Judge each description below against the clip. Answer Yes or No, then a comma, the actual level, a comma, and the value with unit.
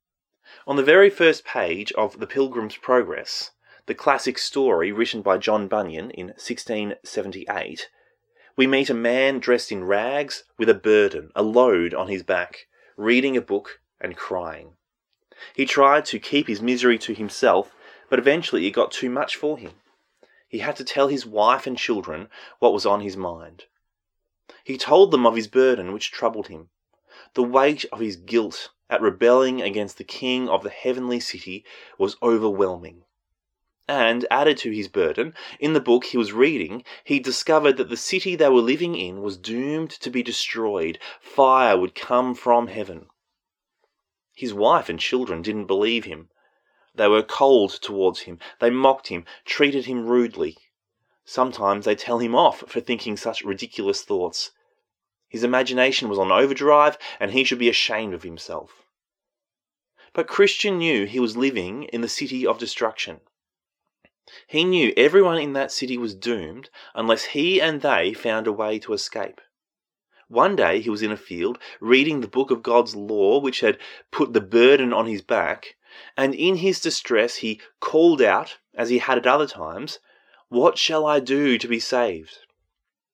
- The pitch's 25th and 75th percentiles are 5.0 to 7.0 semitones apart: No, average, 4.3 semitones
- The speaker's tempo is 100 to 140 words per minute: No, average, 170 wpm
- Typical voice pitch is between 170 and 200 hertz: No, low, 125 Hz